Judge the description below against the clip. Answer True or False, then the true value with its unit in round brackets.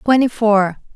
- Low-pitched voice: False (215 Hz)